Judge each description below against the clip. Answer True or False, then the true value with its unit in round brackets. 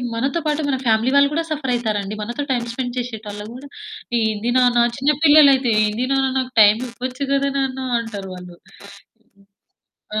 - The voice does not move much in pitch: False (3.6 semitones)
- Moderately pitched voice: False (250 Hz)